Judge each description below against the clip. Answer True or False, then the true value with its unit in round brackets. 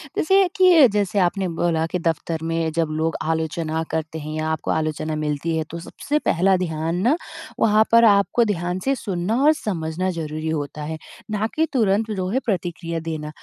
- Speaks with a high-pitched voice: False (170 Hz)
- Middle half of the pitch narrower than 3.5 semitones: False (4.6 semitones)